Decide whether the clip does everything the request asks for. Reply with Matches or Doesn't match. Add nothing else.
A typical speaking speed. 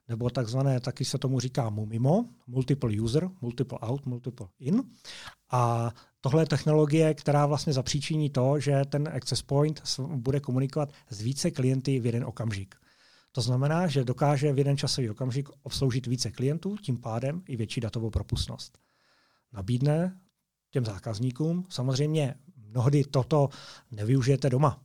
Matches